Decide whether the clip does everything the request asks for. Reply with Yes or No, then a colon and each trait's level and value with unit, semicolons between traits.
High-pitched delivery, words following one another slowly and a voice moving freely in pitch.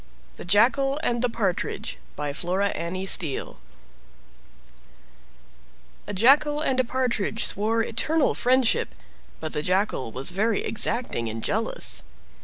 Yes: high, 215 Hz; slow, 120 wpm; wide, 5.8 semitones